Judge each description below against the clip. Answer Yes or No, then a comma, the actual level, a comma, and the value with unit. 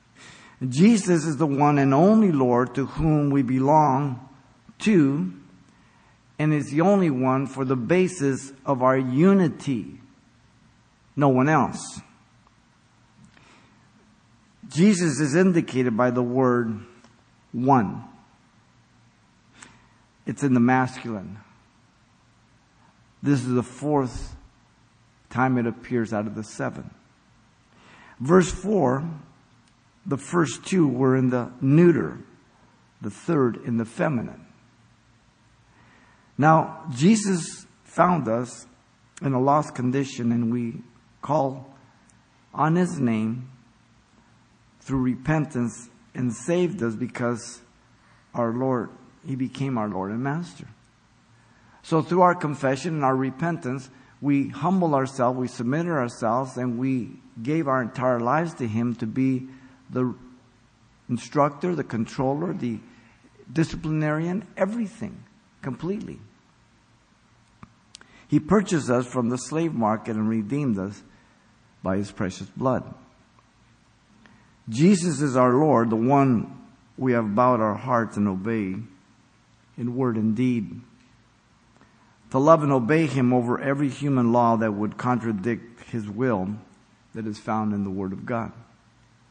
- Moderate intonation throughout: Yes, average, 3.9 semitones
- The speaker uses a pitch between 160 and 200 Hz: No, low, 125 Hz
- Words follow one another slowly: Yes, slow, 115 wpm